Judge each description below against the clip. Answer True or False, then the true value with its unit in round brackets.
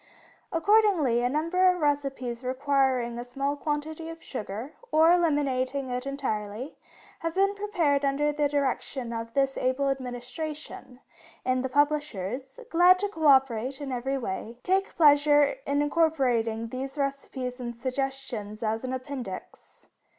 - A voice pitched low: False (275 Hz)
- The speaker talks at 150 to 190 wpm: False (135 wpm)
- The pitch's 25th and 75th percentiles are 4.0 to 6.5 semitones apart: False (3.1 semitones)